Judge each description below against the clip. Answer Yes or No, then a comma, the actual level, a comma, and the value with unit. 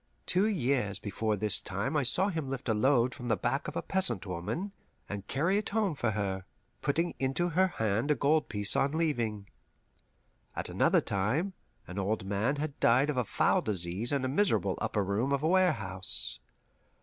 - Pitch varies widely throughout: Yes, wide, 7.2 semitones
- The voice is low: Yes, low, 125 Hz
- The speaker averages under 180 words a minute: No, average, 185 wpm